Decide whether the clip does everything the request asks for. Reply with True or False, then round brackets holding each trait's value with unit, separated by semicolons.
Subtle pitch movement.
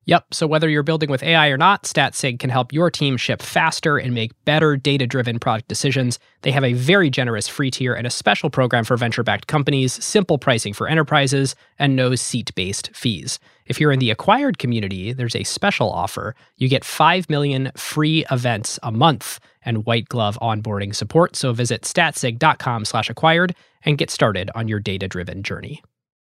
False (4.8 semitones)